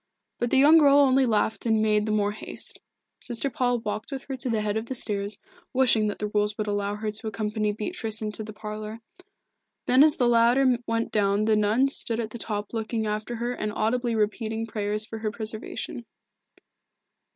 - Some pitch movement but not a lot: No, narrow, 2.2 semitones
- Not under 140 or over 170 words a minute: No, average, 195 wpm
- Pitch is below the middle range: No, high, 220 Hz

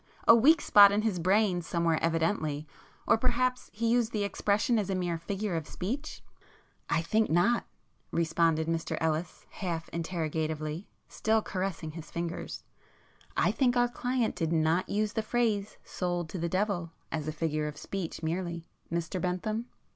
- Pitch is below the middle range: No, medium, 180 Hz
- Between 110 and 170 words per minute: Yes, average, 150 wpm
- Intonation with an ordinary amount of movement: Yes, average, 4.8 semitones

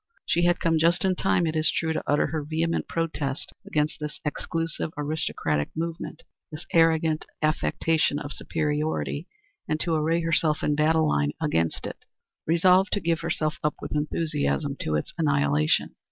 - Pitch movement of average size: No, narrow, 1.8 semitones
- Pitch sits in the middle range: Yes, medium, 155 Hz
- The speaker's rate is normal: Yes, average, 160 wpm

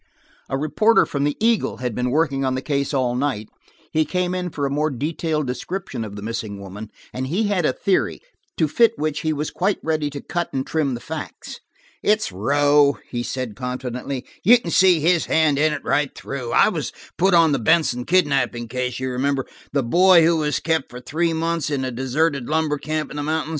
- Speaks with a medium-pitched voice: Yes, medium, 145 Hz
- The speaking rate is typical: No, fast, 210 wpm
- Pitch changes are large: No, average, 4.0 semitones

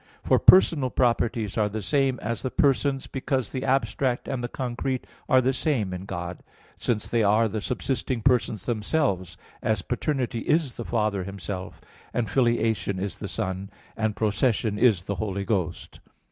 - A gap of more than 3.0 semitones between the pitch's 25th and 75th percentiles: Yes, average, 4.3 semitones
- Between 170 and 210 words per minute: No, average, 160 wpm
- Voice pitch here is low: Yes, low, 115 Hz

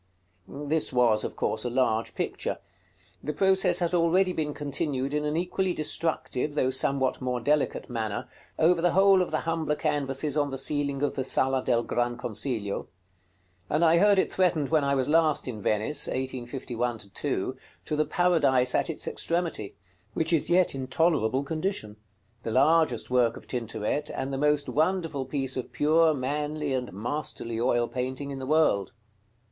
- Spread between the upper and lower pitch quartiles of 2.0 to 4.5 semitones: Yes, average, 4.1 semitones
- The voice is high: No, medium, 140 Hz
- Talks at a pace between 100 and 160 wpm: No, average, 170 wpm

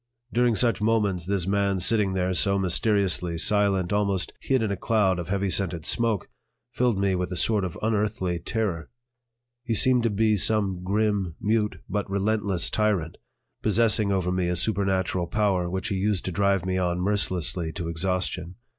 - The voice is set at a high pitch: No, low, 100 Hz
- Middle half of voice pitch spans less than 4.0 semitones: Yes, average, 2.7 semitones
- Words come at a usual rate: Yes, average, 170 wpm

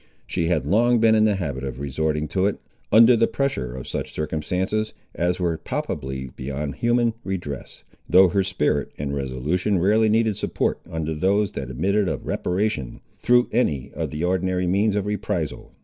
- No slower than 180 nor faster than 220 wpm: No, average, 170 wpm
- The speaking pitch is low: Yes, very low, 90 Hz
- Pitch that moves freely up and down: Yes, wide, 6.0 semitones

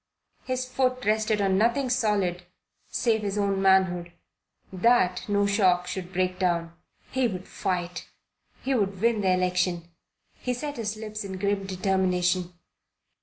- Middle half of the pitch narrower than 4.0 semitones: Yes, average, 3.2 semitones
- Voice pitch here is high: Yes, high, 195 Hz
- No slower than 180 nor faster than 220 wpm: No, average, 140 wpm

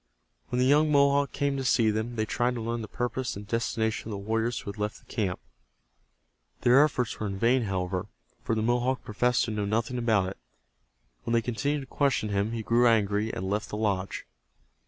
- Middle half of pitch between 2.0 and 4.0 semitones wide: Yes, average, 2.8 semitones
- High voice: No, low, 115 Hz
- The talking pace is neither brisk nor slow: No, fast, 210 wpm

